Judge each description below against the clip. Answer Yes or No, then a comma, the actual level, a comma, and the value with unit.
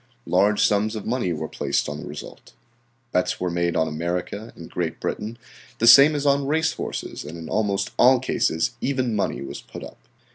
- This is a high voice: No, low, 105 Hz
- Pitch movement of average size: No, wide, 6.5 semitones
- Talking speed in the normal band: Yes, average, 190 wpm